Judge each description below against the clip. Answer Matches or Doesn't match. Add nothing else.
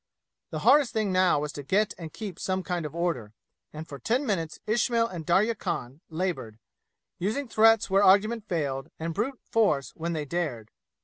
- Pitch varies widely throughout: Matches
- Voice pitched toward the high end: Doesn't match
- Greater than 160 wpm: Matches